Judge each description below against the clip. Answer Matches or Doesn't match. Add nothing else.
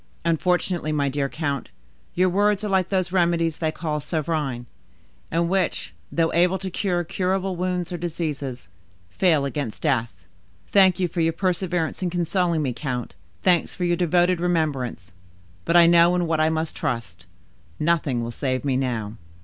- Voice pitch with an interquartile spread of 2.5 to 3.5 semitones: Doesn't match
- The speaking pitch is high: Doesn't match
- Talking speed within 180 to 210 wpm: Doesn't match